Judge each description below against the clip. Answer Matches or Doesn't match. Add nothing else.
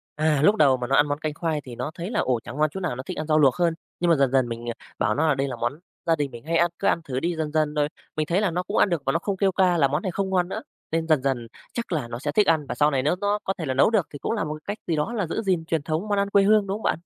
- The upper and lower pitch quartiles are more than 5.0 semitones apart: Doesn't match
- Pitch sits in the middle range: Matches